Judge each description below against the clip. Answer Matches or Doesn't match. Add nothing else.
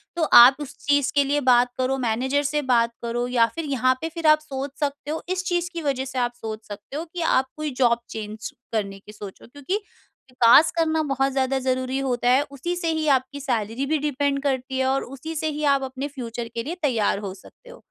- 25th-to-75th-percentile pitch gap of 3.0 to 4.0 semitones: Matches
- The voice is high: Matches